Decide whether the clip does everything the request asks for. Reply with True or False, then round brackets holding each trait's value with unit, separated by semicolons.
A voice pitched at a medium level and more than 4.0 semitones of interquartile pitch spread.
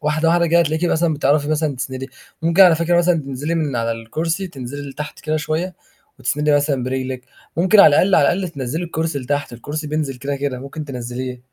False (150 Hz; 3.7 semitones)